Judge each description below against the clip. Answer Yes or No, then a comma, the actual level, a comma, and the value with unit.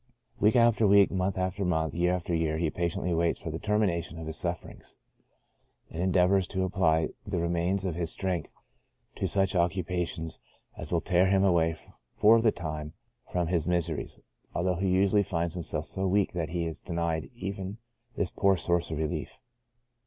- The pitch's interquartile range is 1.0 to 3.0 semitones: Yes, narrow, 2.5 semitones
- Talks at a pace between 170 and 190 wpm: Yes, average, 175 wpm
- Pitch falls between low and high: No, very low, 90 Hz